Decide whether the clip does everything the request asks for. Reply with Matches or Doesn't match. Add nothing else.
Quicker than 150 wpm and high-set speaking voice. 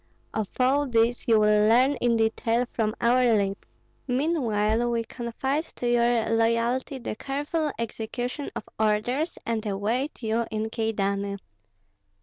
Doesn't match